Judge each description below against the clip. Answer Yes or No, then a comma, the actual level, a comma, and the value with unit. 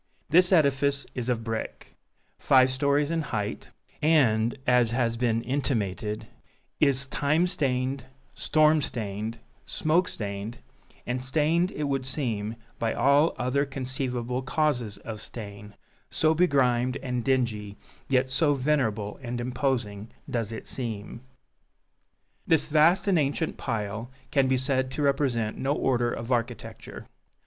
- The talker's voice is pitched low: Yes, low, 130 Hz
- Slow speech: Yes, slow, 130 wpm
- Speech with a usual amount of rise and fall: Yes, average, 3.6 semitones